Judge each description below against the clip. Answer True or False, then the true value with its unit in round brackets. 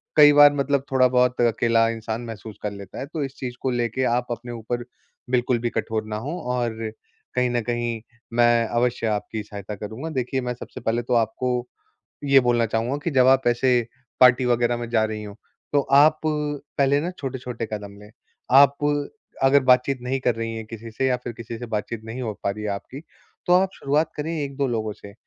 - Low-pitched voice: True (120 Hz)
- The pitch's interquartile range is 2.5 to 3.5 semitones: True (2.9 semitones)